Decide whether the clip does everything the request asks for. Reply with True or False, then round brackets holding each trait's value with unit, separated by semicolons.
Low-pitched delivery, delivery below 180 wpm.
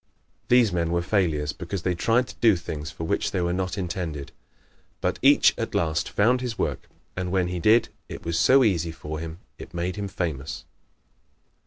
False (90 Hz; 190 wpm)